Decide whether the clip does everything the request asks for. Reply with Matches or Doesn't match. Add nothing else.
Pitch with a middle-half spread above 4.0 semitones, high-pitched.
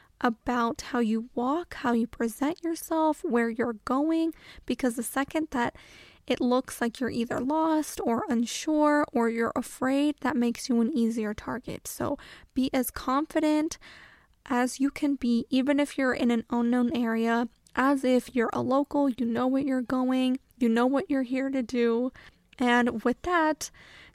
Doesn't match